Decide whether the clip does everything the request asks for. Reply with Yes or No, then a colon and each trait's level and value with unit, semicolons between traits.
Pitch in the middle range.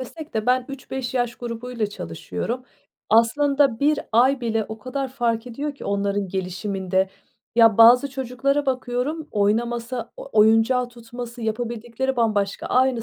No: high, 240 Hz